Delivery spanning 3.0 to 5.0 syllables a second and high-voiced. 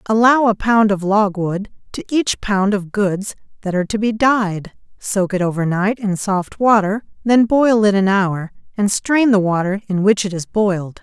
Yes: 4.4 syllables/s; high, 205 Hz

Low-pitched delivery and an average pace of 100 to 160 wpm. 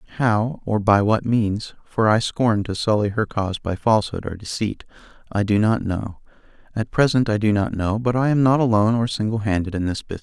No: low, 110 Hz; fast, 205 wpm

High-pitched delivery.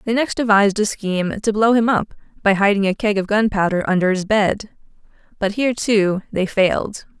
Yes: high, 205 Hz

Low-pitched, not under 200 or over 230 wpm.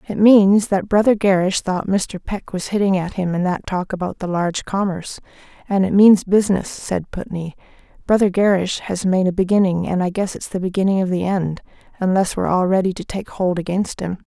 No: high, 190 Hz; fast, 205 wpm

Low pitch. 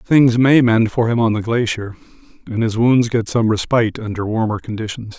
Yes: low, 115 Hz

